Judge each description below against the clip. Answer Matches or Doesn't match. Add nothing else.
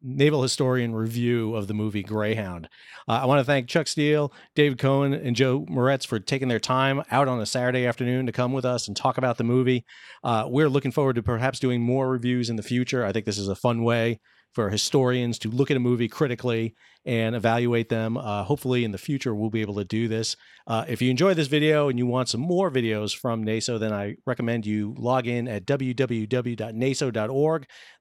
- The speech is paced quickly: Matches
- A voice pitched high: Doesn't match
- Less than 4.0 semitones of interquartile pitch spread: Matches